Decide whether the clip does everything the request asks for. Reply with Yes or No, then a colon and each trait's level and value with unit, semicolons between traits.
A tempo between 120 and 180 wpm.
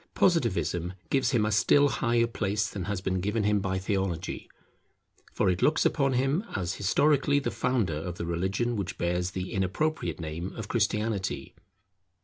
Yes: average, 160 wpm